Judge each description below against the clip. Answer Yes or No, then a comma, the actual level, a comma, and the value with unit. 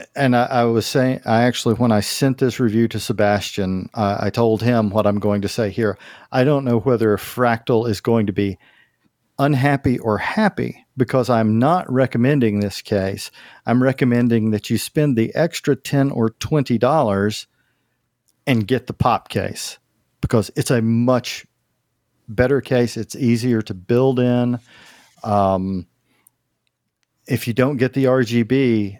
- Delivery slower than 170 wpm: Yes, average, 155 wpm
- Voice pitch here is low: Yes, low, 120 Hz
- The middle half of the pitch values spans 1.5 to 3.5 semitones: Yes, average, 3.0 semitones